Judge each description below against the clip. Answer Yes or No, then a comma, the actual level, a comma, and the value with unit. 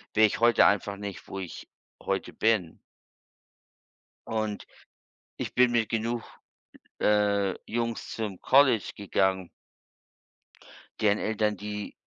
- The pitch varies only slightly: Yes, narrow, 2.0 semitones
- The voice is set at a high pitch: No, low, 105 Hz